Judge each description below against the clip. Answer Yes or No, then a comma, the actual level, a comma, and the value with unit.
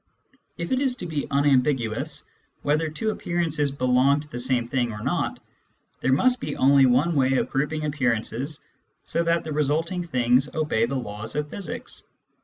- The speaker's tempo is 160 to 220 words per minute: Yes, average, 170 wpm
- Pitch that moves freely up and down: No, average, 3.9 semitones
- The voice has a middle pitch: Yes, medium, 145 Hz